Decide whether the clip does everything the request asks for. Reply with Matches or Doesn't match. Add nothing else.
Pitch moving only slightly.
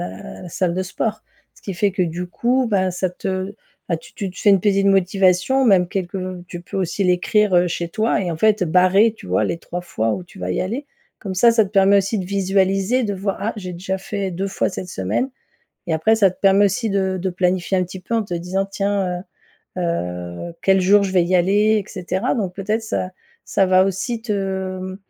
Matches